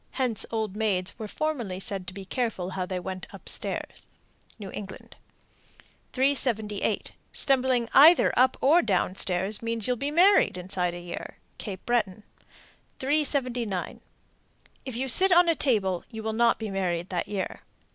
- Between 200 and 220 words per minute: No, average, 155 wpm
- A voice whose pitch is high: Yes, high, 220 Hz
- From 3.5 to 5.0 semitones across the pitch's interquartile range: No, wide, 5.4 semitones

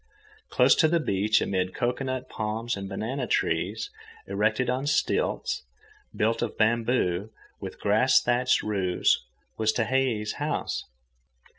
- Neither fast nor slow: No, slow, 125 wpm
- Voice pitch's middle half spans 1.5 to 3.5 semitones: Yes, average, 3.2 semitones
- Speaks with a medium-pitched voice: No, low, 110 Hz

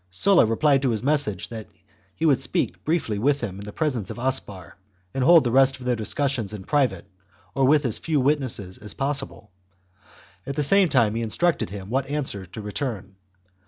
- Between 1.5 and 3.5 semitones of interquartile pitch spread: No, average, 5.3 semitones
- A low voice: Yes, low, 130 Hz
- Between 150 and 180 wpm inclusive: No, average, 195 wpm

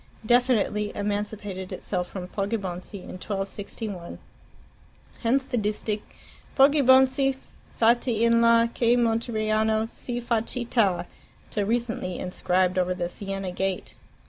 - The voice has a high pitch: Yes, high, 215 Hz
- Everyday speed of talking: No, slow, 110 wpm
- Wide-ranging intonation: No, average, 3.5 semitones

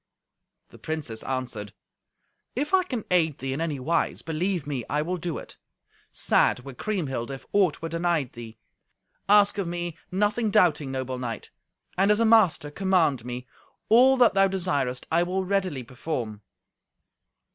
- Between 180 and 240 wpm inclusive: No, average, 155 wpm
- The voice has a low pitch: No, medium, 165 Hz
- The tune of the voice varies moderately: No, wide, 6.7 semitones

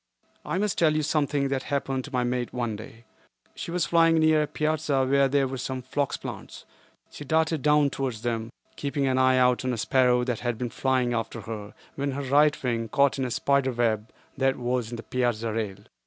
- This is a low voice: Yes, low, 130 Hz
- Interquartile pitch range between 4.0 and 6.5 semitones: No, average, 2.9 semitones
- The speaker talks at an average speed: No, fast, 215 wpm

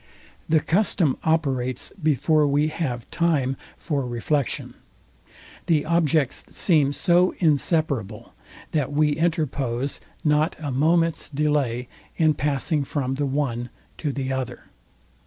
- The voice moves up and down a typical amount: Yes, average, 3.2 semitones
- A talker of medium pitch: Yes, medium, 145 Hz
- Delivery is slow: Yes, slow, 115 wpm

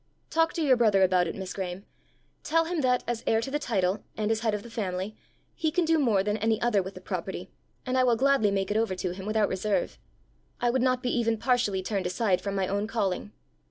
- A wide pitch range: No, average, 4.4 semitones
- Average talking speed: No, fast, 240 wpm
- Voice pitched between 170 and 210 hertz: No, high, 220 Hz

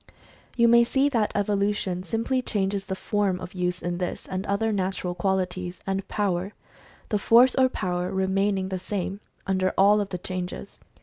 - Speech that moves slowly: No, average, 180 wpm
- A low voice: No, high, 195 Hz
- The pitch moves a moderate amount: No, narrow, 2.1 semitones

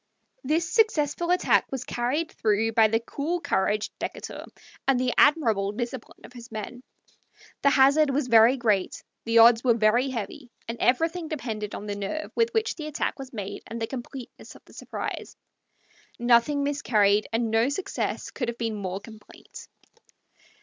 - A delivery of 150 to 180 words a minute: Yes, average, 165 wpm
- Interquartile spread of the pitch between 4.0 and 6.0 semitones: Yes, average, 4.5 semitones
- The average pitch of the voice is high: Yes, high, 240 Hz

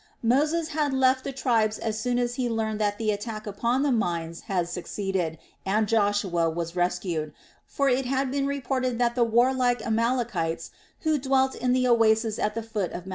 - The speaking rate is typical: Yes, average, 185 wpm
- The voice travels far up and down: No, average, 4.1 semitones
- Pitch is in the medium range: No, high, 230 Hz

